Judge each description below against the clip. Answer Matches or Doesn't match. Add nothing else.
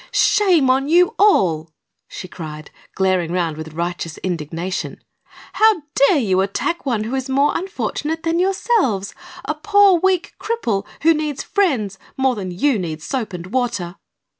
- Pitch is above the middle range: Matches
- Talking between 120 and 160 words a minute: Matches